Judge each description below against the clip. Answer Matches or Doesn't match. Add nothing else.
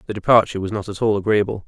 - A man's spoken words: Matches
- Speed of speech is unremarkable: Doesn't match